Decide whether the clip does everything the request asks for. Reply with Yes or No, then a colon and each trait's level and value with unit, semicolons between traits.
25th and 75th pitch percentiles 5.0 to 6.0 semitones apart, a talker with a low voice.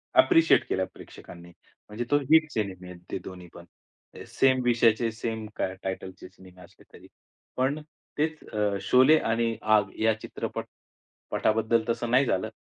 Yes: average, 5.3 semitones; low, 110 Hz